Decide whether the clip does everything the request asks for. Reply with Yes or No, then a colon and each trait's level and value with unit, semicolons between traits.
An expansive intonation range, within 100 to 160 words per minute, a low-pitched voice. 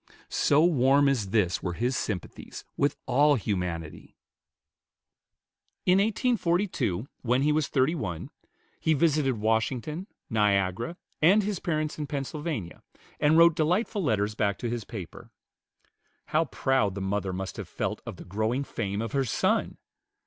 Yes: wide, 7.0 semitones; average, 140 wpm; low, 130 Hz